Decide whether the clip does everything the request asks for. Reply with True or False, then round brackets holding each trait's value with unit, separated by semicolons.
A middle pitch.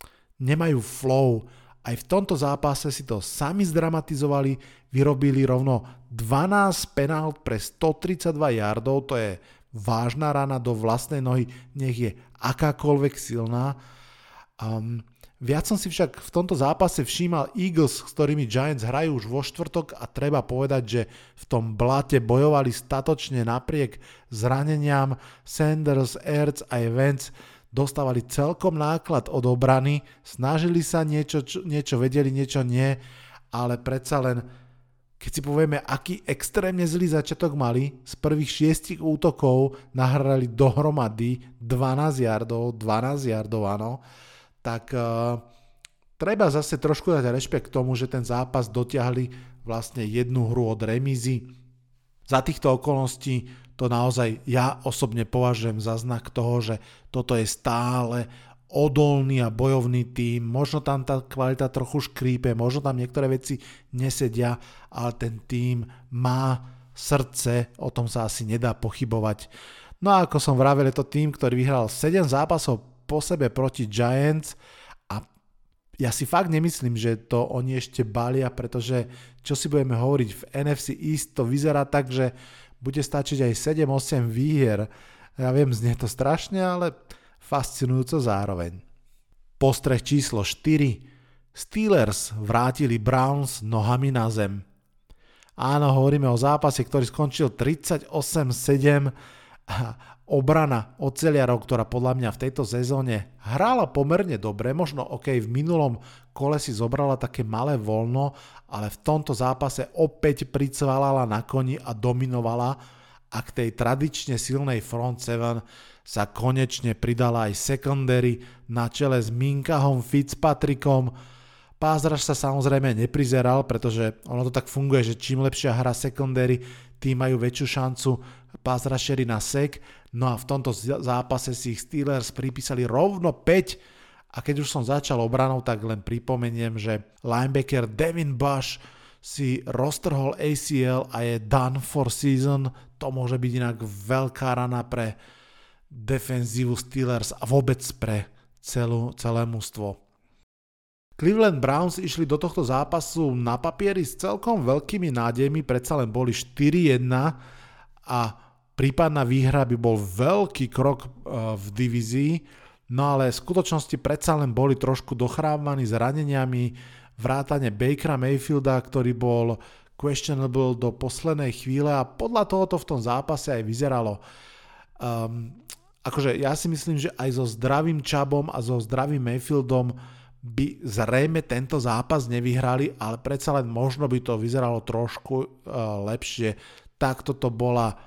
False (130 Hz)